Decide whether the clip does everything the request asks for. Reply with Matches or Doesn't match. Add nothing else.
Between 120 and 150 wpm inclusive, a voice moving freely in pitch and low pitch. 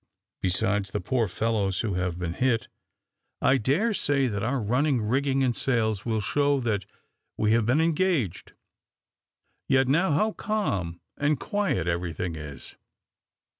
Matches